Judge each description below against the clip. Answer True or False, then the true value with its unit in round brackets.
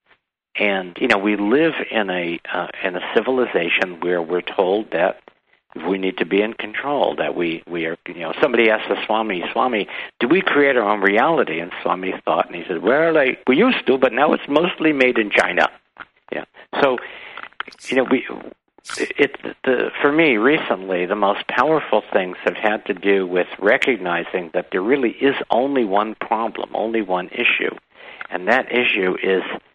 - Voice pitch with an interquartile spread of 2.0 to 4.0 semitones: False (4.7 semitones)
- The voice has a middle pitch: False (100 Hz)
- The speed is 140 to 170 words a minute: False (185 wpm)